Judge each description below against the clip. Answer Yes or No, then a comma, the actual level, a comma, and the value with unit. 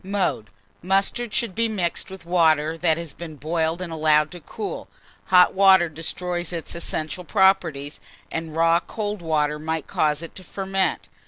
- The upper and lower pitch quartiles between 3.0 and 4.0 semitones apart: Yes, average, 3.3 semitones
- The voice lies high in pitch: No, medium, 170 Hz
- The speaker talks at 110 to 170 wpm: Yes, average, 160 wpm